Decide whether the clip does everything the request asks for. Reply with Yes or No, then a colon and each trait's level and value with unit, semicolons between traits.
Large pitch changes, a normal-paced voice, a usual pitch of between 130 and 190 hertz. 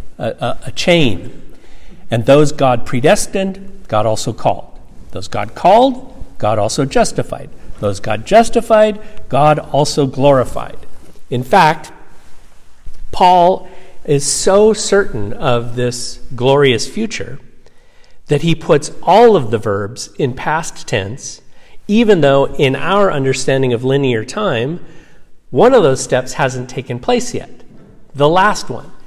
No: wide, 6.9 semitones; slow, 125 wpm; medium, 140 Hz